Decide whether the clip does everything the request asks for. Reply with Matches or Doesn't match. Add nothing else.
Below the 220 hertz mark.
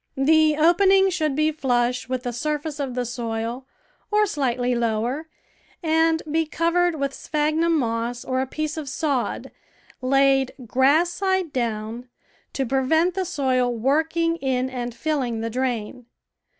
Doesn't match